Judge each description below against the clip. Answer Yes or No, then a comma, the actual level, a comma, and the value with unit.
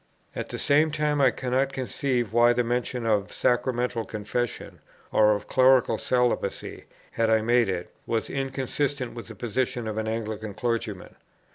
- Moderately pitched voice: No, low, 120 Hz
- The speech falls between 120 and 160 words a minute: Yes, average, 155 wpm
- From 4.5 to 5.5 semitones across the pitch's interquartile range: No, average, 2.7 semitones